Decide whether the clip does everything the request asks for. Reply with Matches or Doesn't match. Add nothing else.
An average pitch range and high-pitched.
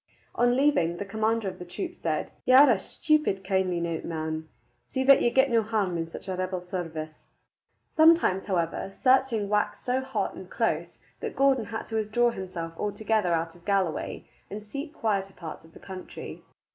Doesn't match